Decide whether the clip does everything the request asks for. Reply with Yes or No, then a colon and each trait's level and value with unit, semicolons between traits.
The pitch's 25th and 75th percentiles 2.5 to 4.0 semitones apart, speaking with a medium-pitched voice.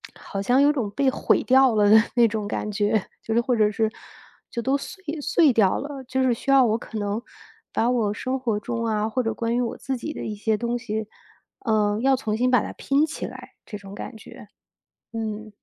No: average, 3.4 semitones; high, 230 Hz